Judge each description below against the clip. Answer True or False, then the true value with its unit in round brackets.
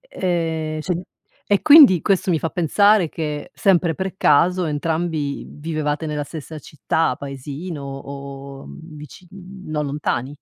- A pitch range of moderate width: True (3.3 semitones)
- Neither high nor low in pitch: True (155 Hz)